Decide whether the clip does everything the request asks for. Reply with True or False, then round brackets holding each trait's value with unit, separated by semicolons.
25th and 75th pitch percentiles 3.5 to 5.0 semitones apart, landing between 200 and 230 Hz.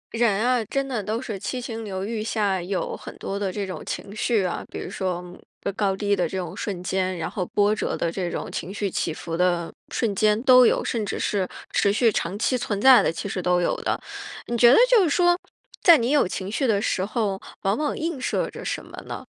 True (4.1 semitones; 205 Hz)